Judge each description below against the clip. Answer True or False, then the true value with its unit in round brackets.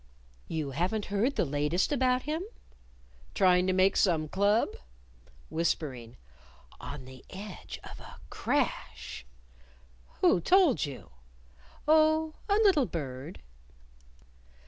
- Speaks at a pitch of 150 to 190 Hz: True (185 Hz)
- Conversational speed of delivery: False (105 wpm)